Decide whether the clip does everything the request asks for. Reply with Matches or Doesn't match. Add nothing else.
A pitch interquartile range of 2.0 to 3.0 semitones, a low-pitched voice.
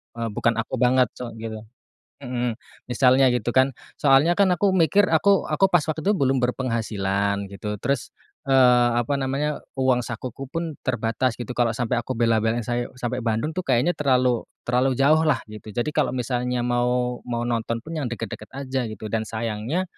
Matches